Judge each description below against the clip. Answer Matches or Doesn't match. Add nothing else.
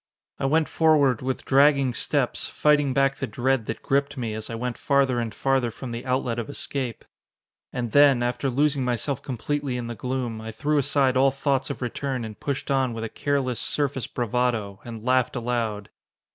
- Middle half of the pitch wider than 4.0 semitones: Doesn't match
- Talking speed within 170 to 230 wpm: Matches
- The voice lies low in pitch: Matches